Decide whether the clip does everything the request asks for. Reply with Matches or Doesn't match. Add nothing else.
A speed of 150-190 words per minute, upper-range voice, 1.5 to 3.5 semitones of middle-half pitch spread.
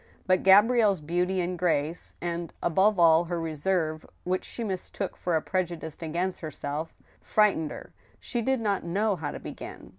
Doesn't match